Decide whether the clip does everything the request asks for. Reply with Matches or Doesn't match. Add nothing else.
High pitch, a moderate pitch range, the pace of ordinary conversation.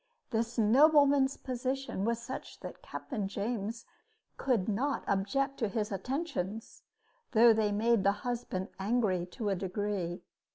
Doesn't match